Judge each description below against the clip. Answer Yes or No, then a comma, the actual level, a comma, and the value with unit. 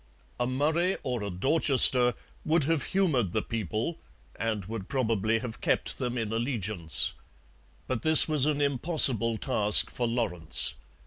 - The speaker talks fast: No, average, 140 wpm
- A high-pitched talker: No, low, 120 Hz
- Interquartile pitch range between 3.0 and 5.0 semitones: Yes, average, 4.7 semitones